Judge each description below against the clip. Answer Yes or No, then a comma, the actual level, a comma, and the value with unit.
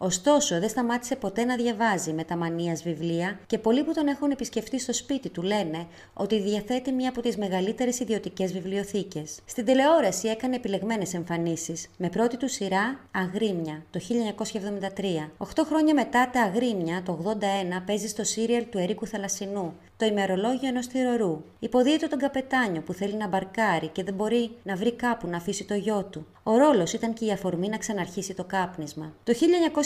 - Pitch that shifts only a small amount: No, average, 4.5 semitones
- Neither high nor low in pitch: No, high, 210 Hz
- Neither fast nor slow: No, fast, 175 wpm